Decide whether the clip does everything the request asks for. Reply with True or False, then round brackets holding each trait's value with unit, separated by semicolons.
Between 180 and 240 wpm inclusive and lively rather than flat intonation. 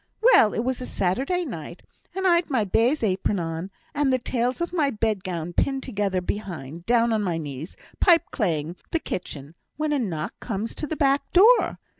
True (185 wpm; 7.7 semitones)